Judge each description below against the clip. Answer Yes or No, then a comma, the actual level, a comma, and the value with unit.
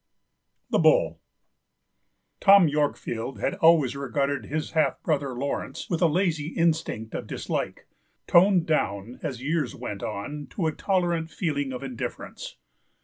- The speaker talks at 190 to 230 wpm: No, slow, 135 wpm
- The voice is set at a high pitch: No, medium, 150 Hz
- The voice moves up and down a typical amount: Yes, average, 3.8 semitones